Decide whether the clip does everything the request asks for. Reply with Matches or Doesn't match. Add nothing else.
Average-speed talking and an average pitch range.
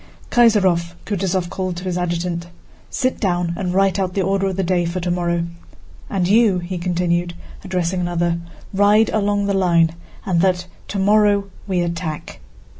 Doesn't match